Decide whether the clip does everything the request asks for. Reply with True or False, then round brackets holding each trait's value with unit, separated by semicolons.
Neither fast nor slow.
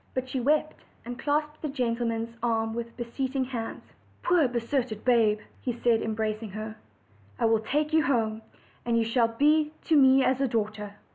True (170 wpm)